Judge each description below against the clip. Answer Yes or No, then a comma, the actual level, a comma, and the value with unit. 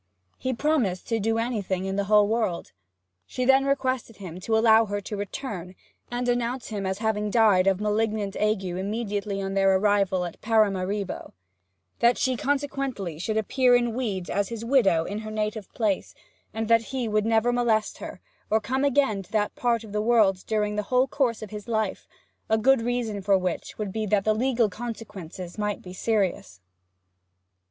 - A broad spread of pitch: No, average, 3.1 semitones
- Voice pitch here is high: Yes, high, 215 Hz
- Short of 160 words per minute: No, average, 180 wpm